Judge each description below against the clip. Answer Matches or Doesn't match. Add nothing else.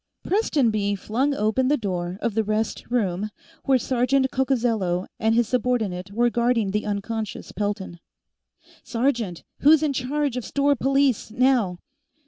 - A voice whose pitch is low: Doesn't match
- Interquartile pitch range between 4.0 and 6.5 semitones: Matches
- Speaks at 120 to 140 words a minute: Matches